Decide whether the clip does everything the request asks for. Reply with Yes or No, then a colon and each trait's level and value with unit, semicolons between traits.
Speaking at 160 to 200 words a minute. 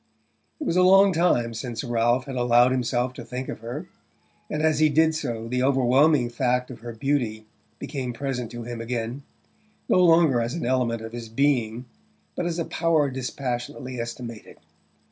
Yes: average, 175 wpm